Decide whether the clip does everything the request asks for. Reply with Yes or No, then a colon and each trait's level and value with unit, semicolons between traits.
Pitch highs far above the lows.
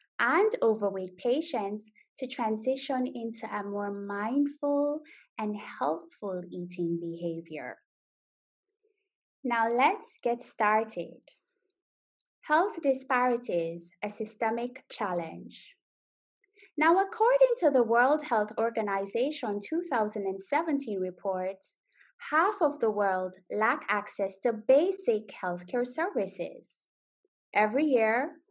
Yes: wide, 6.5 semitones